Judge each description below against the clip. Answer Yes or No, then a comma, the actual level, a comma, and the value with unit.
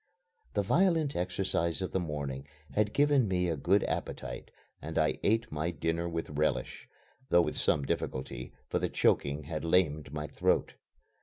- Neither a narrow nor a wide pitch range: Yes, average, 4.3 semitones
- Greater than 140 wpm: Yes, average, 160 wpm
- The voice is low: Yes, very low, 85 Hz